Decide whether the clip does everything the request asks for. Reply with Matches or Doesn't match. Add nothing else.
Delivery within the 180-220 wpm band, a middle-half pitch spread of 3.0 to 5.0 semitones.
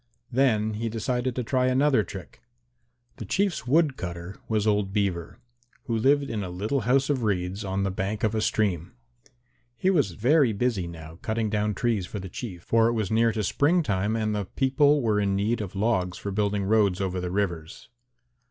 Matches